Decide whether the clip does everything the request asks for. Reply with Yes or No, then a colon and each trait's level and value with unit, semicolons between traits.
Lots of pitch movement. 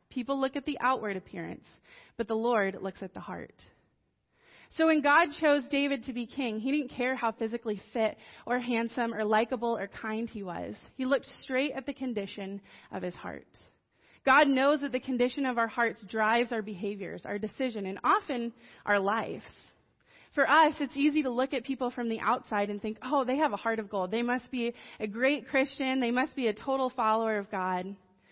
No: average, 3.8 semitones